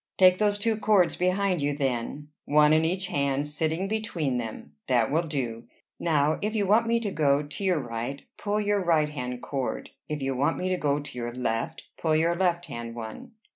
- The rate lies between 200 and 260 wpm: Yes, fast, 205 wpm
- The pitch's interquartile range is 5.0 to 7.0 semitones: Yes, wide, 5.5 semitones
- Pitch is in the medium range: Yes, medium, 150 Hz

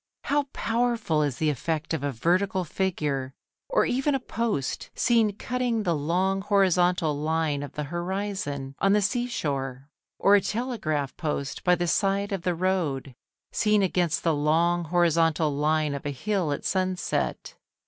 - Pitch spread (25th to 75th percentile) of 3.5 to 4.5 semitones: No, average, 5.1 semitones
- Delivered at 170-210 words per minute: No, average, 160 wpm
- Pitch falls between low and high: Yes, medium, 175 Hz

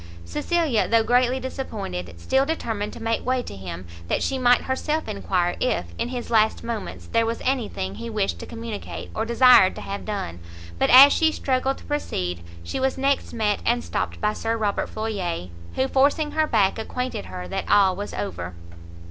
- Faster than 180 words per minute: Yes, average, 190 wpm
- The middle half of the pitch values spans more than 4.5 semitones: Yes, average, 5.2 semitones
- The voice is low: No, high, 225 Hz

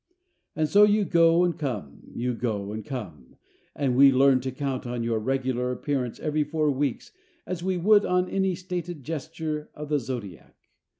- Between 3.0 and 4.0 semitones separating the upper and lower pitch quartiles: No, average, 5.1 semitones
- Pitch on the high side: No, medium, 140 Hz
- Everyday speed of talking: Yes, average, 175 wpm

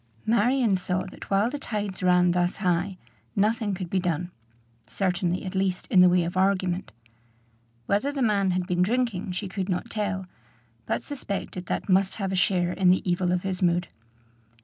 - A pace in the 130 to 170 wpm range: No, average, 180 wpm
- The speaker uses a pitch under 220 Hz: Yes, medium, 185 Hz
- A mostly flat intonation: Yes, narrow, 2.1 semitones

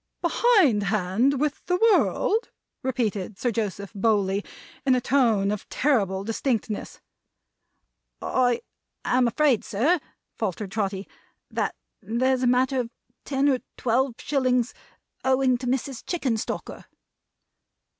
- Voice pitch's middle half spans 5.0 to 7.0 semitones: No, average, 4.3 semitones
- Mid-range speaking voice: No, high, 245 Hz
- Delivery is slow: Yes, slow, 115 wpm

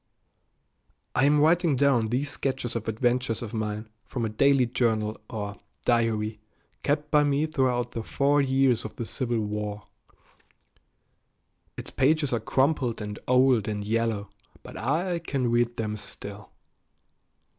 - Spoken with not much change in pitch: No, average, 4.1 semitones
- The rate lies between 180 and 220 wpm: No, average, 140 wpm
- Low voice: Yes, low, 120 Hz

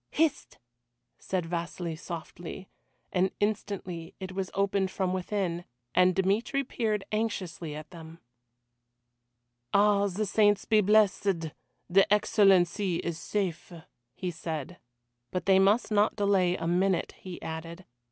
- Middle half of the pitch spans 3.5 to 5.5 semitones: No, average, 2.9 semitones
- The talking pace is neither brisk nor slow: No, slow, 125 wpm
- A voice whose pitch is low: No, high, 190 Hz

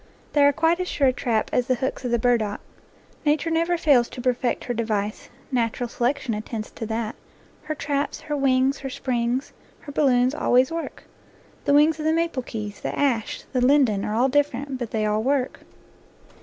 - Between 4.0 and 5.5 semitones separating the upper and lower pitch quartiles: No, average, 3.5 semitones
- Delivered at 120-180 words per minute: No, average, 195 wpm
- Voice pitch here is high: Yes, very high, 255 Hz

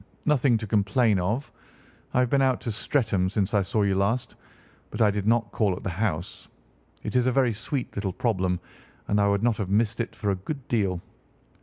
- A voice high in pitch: No, low, 105 Hz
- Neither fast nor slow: No, fast, 210 wpm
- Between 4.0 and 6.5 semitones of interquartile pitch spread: No, average, 3.5 semitones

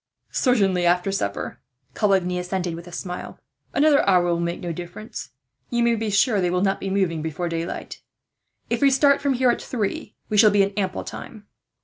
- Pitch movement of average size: Yes, average, 3.9 semitones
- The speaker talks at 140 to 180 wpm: No, average, 195 wpm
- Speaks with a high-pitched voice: Yes, high, 195 Hz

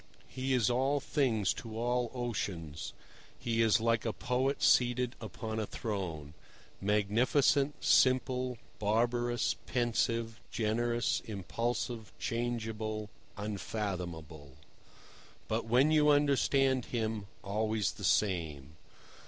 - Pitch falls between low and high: No, low, 115 Hz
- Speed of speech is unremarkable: No, slow, 95 wpm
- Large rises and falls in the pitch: No, average, 3.0 semitones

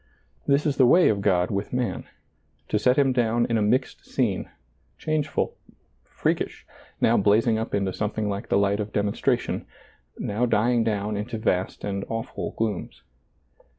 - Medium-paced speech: Yes, average, 165 wpm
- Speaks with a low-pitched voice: Yes, low, 110 Hz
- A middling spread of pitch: Yes, average, 3.3 semitones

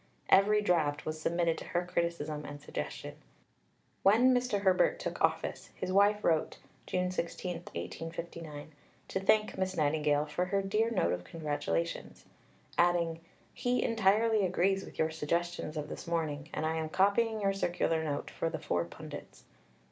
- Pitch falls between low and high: Yes, medium, 170 Hz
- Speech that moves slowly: No, average, 155 wpm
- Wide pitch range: No, average, 4.0 semitones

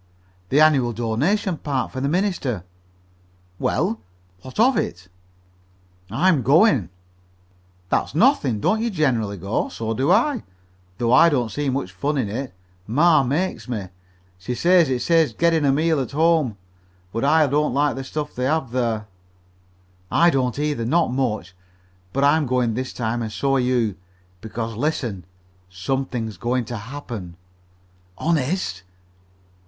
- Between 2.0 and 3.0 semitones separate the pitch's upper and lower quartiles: No, average, 5.2 semitones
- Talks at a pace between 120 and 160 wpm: Yes, average, 145 wpm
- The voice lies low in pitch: Yes, low, 130 Hz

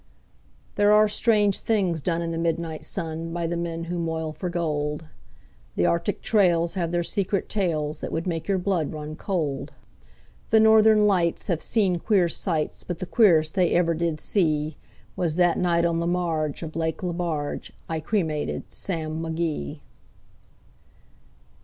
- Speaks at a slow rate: No, average, 160 wpm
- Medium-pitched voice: Yes, medium, 170 Hz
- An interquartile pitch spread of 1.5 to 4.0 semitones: Yes, narrow, 2.4 semitones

